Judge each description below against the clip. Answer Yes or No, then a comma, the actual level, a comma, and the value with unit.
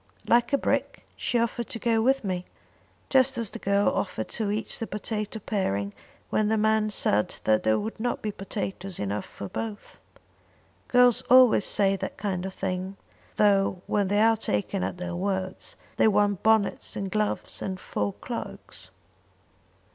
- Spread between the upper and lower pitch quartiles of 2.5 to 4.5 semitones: Yes, average, 2.9 semitones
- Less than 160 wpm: No, average, 165 wpm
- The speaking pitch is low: No, high, 205 Hz